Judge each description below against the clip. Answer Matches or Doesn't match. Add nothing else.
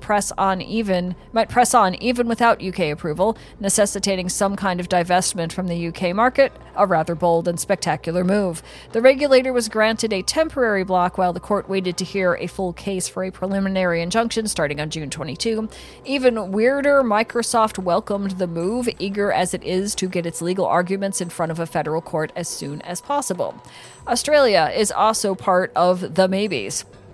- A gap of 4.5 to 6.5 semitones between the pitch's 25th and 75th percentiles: Doesn't match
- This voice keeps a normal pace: Matches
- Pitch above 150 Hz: Matches